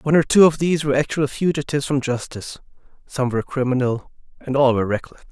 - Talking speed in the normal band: Yes, average, 190 wpm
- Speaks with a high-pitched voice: No, low, 135 Hz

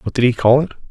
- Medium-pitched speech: No, low, 130 Hz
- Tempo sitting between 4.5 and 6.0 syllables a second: No, 7.8 syllables/s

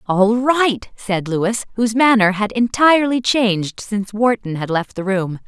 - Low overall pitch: No, high, 215 Hz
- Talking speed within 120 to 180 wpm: Yes, average, 165 wpm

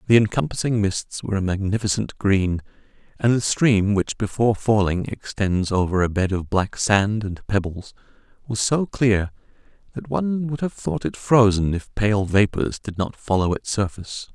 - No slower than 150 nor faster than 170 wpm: Yes, average, 165 wpm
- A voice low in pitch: Yes, low, 105 Hz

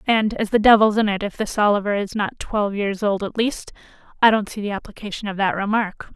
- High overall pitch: Yes, high, 210 Hz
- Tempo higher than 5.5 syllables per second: Yes, 5.9 syllables/s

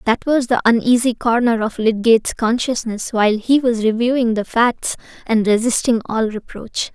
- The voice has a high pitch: Yes, high, 230 Hz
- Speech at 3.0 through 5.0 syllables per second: Yes, 4.8 syllables/s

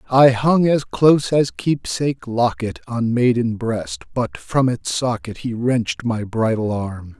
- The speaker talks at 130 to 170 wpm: Yes, average, 150 wpm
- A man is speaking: Yes, male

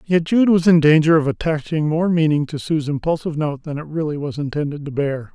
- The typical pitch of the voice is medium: Yes, medium, 155 Hz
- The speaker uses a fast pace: Yes, fast, 225 wpm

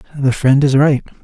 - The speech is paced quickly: No, average, 195 wpm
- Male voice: Yes, male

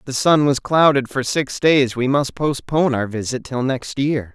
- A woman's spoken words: No, male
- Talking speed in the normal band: No, fast, 220 wpm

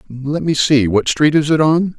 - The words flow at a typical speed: No, fast, 240 wpm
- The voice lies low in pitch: No, medium, 145 Hz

